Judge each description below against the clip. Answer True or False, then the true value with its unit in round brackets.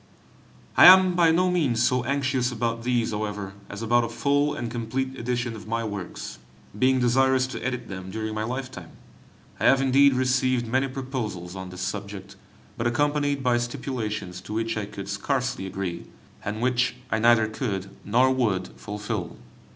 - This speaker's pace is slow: False (165 wpm)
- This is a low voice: True (120 Hz)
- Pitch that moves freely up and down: False (3.7 semitones)